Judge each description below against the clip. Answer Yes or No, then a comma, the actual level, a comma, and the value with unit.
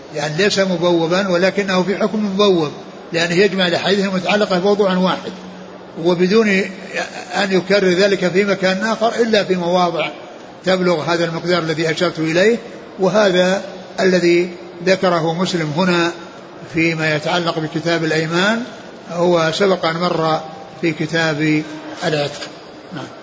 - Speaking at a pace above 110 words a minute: Yes, average, 120 wpm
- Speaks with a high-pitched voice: No, medium, 180 Hz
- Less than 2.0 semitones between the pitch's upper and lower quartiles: No, narrow, 2.6 semitones